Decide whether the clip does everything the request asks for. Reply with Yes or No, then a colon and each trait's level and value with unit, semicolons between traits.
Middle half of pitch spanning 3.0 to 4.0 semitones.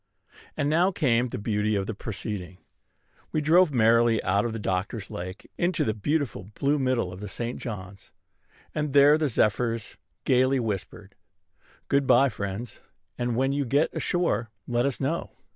No: average, 5.1 semitones